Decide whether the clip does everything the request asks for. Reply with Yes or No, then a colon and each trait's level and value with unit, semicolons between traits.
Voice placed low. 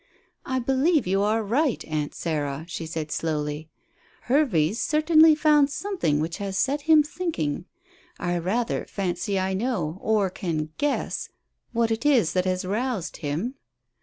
No: high, 200 Hz